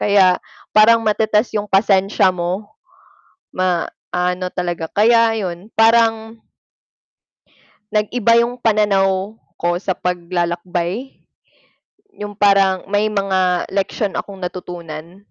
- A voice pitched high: Yes, high, 195 Hz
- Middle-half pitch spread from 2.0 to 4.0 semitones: Yes, average, 3.1 semitones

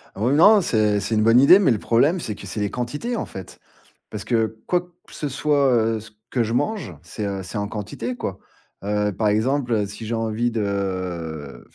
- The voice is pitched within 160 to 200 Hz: No, low, 110 Hz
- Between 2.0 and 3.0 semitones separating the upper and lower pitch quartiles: No, average, 3.8 semitones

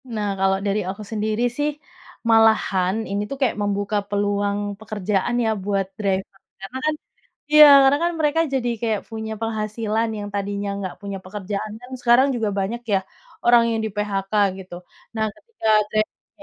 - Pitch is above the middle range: Yes, high, 215 Hz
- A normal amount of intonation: No, narrow, 2.3 semitones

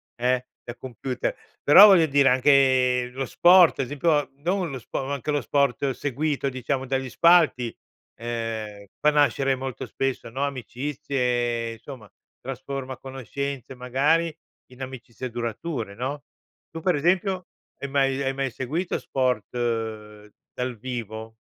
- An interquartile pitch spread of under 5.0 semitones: Yes, average, 2.8 semitones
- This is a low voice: Yes, low, 130 Hz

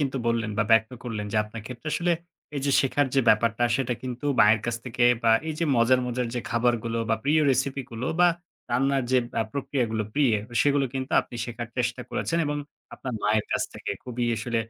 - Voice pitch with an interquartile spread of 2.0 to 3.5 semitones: Yes, average, 2.8 semitones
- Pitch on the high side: No, low, 120 Hz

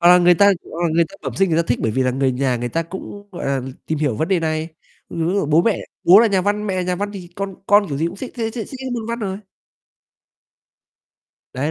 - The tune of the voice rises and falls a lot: No, average, 4.6 semitones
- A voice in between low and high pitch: Yes, medium, 175 Hz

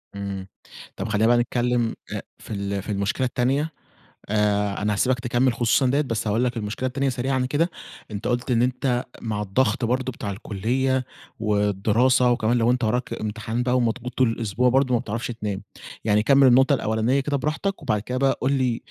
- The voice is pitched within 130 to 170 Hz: No, low, 120 Hz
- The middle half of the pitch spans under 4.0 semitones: Yes, average, 3.3 semitones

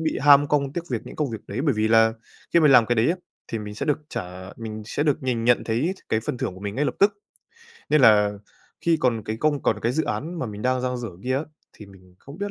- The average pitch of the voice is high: No, low, 125 Hz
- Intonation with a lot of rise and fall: No, average, 5.0 semitones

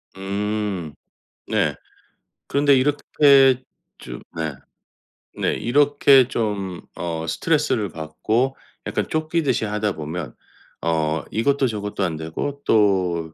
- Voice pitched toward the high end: No, low, 105 Hz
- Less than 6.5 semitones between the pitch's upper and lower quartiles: No, wide, 8.3 semitones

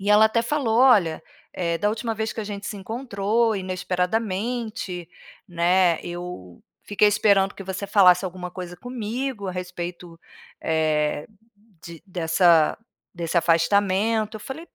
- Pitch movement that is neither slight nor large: Yes, average, 3.9 semitones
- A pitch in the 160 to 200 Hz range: Yes, high, 190 Hz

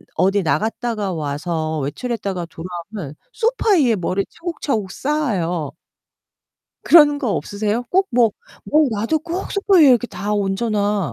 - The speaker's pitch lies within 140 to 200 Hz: No, high, 210 Hz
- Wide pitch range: Yes, wide, 8.1 semitones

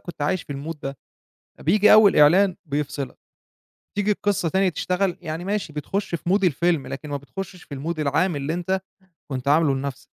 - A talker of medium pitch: Yes, medium, 165 Hz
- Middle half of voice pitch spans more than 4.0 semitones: Yes, average, 4.8 semitones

